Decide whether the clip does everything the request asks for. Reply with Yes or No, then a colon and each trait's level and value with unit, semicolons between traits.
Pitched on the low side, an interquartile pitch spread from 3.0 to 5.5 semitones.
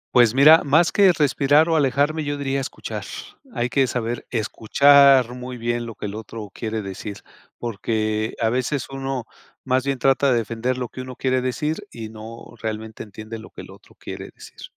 Yes: low, 125 Hz; average, 3.7 semitones